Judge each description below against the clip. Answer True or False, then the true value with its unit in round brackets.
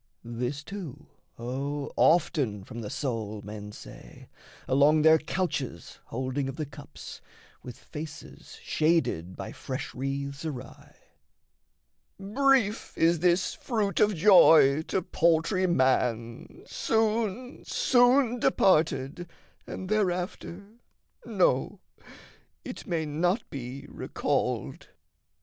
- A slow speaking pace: True (100 wpm)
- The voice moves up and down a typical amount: False (6.3 semitones)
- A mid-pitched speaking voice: True (155 Hz)